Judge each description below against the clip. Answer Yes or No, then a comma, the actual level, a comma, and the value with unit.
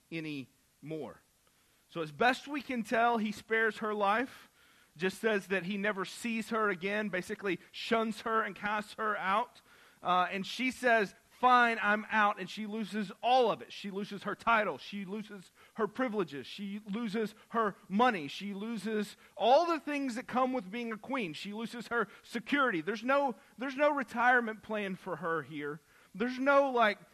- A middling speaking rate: Yes, average, 175 wpm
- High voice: Yes, high, 215 Hz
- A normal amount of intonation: Yes, average, 3.0 semitones